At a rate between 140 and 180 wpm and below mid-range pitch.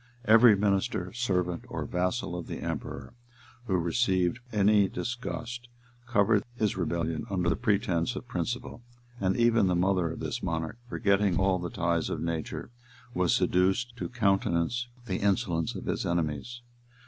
Yes: average, 150 wpm; very low, 95 Hz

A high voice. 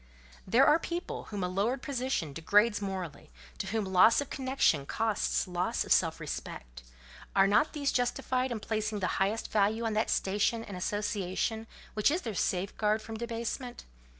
Yes: high, 215 Hz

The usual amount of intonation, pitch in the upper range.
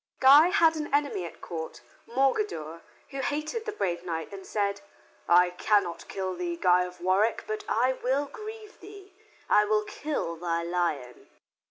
No: wide, 8.8 semitones; high, 210 Hz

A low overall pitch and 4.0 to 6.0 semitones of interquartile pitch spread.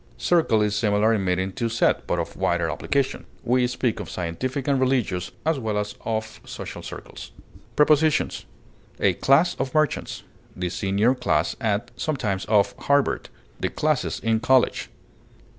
Yes: low, 115 Hz; average, 4.6 semitones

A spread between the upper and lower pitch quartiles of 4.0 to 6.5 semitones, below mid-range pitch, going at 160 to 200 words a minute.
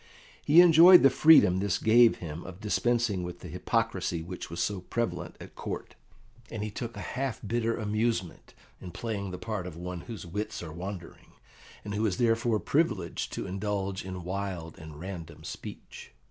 Yes: average, 4.4 semitones; low, 100 Hz; average, 175 wpm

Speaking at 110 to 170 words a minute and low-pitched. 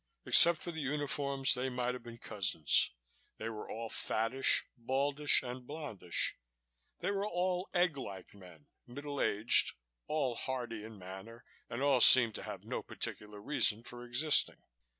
Yes: average, 150 wpm; low, 125 Hz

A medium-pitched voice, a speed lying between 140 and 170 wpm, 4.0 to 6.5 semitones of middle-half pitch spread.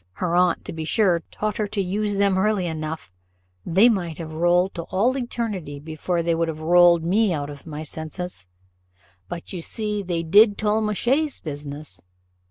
No: medium, 175 Hz; average, 180 wpm; average, 4.6 semitones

